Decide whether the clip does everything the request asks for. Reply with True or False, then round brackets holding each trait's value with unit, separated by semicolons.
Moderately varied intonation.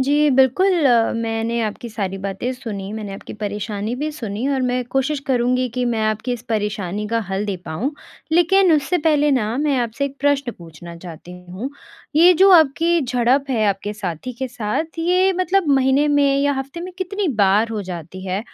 False (5.9 semitones)